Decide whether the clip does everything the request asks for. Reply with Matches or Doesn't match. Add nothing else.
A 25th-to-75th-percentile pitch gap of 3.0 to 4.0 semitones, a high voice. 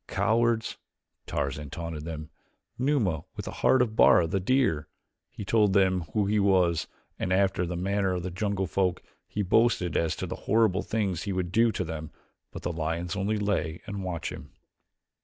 Doesn't match